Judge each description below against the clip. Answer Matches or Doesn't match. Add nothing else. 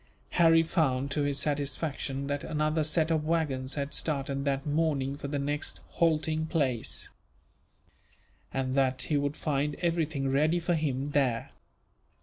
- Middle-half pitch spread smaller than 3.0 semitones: Matches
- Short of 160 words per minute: Matches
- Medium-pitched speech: Matches